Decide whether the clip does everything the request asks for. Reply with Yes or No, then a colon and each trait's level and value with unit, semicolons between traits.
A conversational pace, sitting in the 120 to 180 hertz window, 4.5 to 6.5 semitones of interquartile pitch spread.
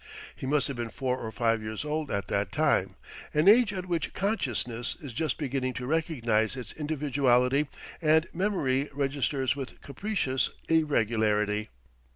Yes: average, 150 wpm; low, 135 Hz; average, 4.8 semitones